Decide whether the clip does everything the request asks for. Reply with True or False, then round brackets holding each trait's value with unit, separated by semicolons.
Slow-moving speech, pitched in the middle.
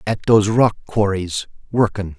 False (110 wpm; 105 Hz)